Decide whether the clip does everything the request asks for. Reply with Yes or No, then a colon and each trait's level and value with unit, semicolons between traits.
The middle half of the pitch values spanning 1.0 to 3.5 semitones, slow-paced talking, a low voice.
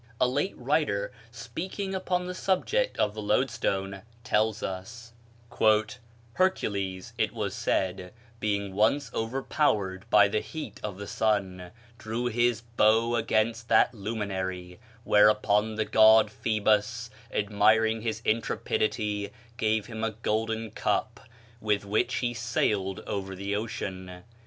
Yes: narrow, 2.4 semitones; slow, 125 wpm; low, 110 Hz